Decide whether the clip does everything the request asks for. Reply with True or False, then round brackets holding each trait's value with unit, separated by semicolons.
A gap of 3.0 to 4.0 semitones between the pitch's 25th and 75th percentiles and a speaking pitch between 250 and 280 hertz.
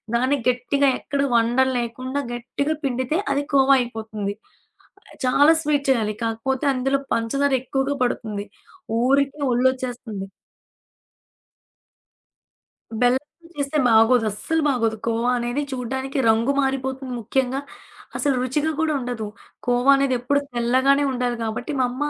False (2.6 semitones; 255 Hz)